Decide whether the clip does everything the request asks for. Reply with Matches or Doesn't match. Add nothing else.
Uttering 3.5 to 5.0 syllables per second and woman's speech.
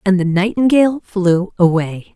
Matches